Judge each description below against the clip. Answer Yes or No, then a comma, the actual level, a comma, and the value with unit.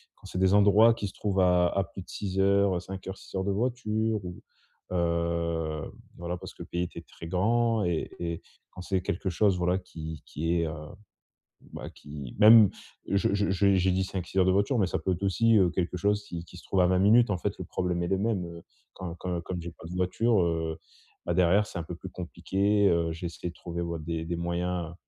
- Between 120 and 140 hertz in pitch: No, very low, 90 Hz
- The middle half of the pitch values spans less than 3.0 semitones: Yes, narrow, 2.6 semitones